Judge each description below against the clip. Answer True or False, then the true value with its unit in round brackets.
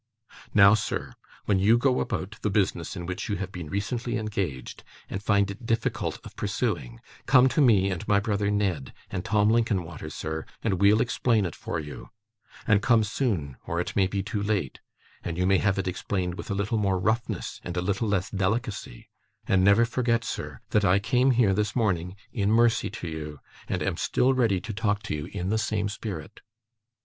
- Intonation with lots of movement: False (3.3 semitones)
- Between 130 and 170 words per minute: False (195 wpm)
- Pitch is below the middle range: True (100 Hz)